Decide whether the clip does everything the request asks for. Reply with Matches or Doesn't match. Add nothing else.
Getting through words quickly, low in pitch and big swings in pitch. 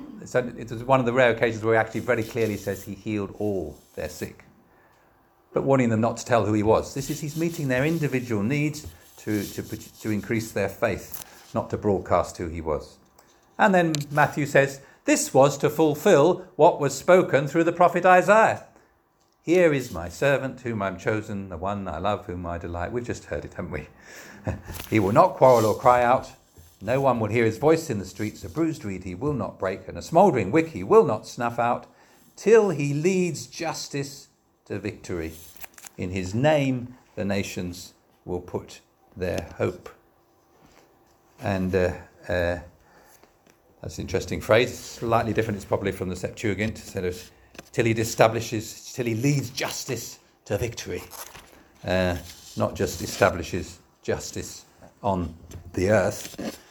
Doesn't match